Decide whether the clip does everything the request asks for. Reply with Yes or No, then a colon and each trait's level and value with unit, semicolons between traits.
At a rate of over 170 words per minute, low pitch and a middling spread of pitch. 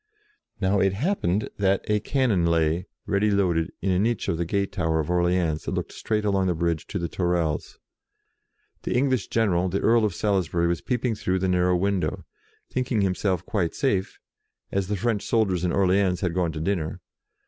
Yes: average, 190 wpm; very low, 95 Hz; average, 3.1 semitones